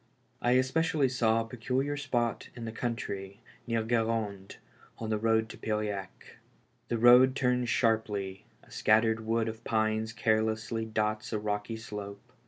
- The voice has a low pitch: Yes, low, 110 Hz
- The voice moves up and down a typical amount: No, narrow, 1.9 semitones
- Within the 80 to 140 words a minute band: No, average, 165 wpm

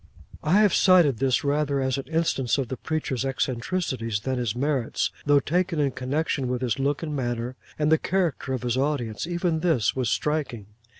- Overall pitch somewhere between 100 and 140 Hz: Yes, low, 135 Hz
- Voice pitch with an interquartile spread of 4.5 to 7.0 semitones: No, average, 4.0 semitones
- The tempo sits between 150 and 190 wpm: Yes, average, 185 wpm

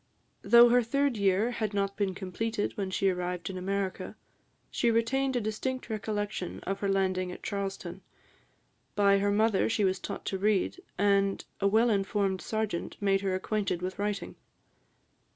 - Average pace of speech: Yes, average, 160 wpm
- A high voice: Yes, high, 200 Hz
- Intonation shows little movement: Yes, narrow, 2.3 semitones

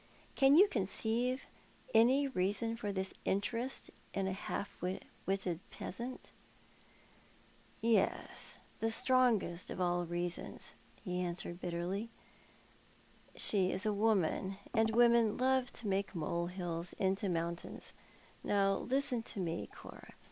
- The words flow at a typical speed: No, slow, 120 wpm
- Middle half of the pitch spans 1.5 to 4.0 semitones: No, average, 4.4 semitones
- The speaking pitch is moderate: No, high, 200 Hz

